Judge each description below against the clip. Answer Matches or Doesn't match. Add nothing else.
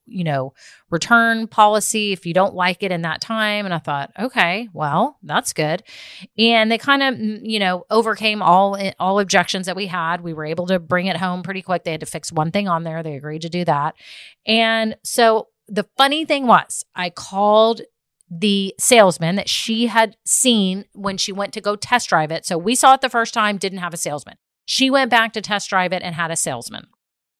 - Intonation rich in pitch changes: Doesn't match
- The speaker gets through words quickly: Matches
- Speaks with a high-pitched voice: Matches